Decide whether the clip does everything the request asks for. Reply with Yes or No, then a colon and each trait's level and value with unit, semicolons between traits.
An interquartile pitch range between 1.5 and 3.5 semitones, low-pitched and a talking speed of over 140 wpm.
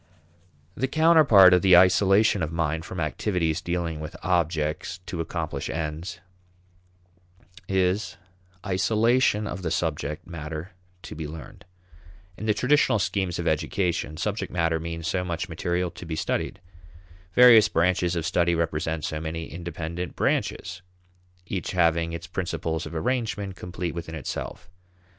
No: average, 2.7 semitones; very low, 85 Hz; slow, 135 wpm